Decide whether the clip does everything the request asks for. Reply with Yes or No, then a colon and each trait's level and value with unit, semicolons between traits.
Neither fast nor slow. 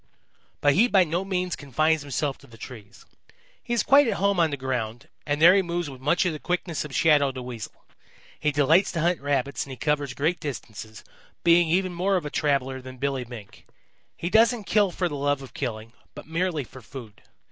No: fast, 210 wpm